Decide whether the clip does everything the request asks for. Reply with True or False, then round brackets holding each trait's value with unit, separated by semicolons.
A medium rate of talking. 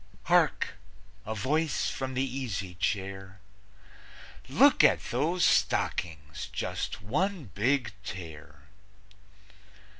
False (90 wpm)